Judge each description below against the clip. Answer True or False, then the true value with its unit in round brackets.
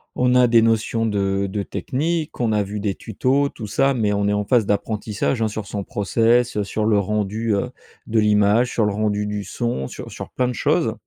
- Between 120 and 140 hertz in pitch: False (105 Hz)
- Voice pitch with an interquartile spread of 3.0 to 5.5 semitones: False (2.5 semitones)